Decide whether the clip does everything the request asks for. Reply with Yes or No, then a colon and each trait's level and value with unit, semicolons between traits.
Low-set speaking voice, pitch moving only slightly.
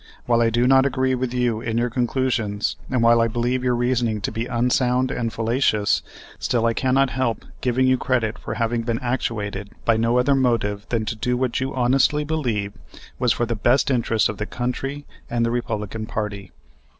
Yes: low, 120 Hz; narrow, 2.2 semitones